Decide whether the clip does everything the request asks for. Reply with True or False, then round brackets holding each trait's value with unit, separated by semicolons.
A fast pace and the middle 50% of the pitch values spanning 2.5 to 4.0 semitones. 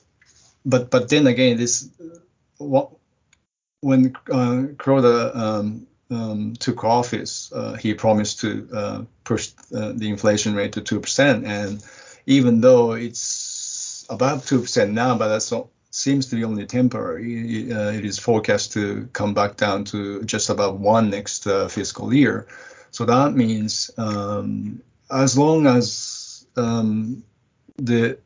False (140 wpm; 3.2 semitones)